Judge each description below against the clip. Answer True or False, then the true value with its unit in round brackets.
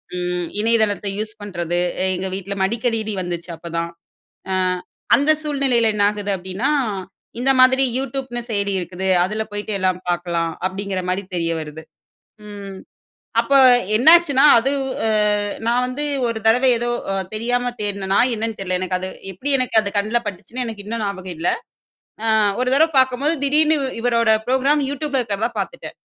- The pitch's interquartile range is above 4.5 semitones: True (5.0 semitones)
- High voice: True (215 Hz)